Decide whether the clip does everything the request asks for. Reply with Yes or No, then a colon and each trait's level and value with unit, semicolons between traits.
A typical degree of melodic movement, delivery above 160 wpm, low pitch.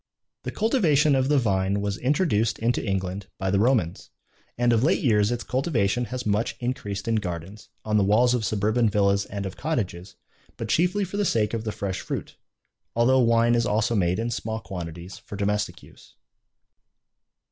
Yes: average, 3.6 semitones; average, 180 wpm; low, 110 Hz